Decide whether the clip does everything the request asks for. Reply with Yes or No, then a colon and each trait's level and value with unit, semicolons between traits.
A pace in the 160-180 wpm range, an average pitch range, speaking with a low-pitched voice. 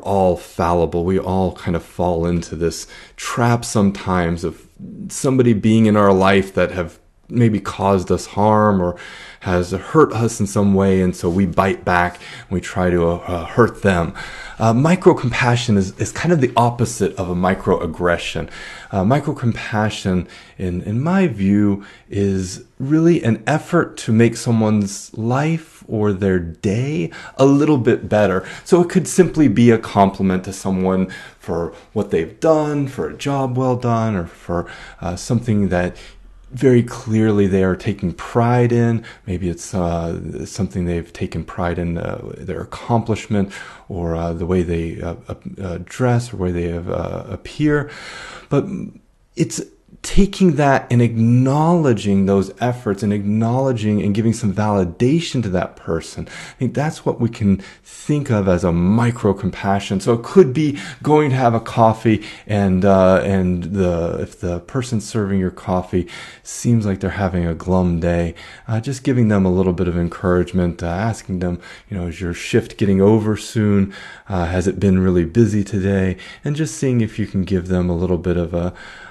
Yes: average, 170 wpm; average, 4.7 semitones; low, 100 Hz